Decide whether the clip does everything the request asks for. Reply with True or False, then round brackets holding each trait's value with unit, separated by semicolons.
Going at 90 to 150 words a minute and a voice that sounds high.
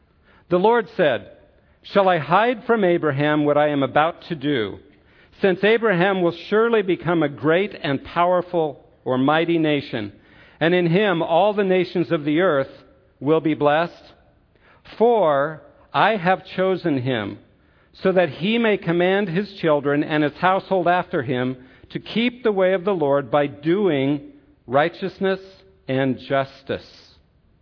False (145 wpm; 165 Hz)